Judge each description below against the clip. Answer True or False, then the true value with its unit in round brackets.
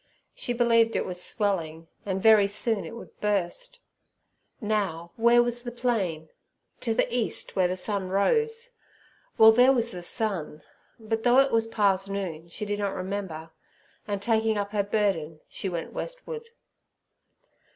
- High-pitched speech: True (205 Hz)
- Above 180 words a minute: False (155 wpm)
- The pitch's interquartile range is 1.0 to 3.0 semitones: False (3.9 semitones)